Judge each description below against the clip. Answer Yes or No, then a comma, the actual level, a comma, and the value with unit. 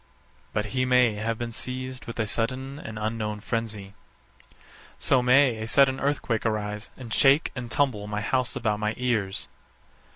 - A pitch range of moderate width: Yes, average, 3.2 semitones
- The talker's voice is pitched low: Yes, low, 115 Hz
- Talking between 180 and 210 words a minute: No, average, 165 wpm